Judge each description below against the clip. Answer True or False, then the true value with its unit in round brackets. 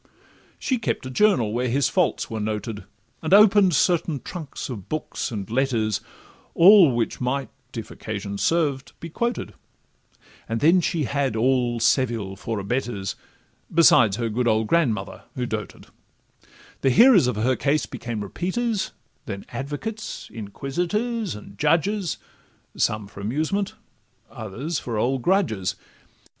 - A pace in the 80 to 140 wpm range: True (135 wpm)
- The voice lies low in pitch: True (130 Hz)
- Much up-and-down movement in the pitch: True (7.3 semitones)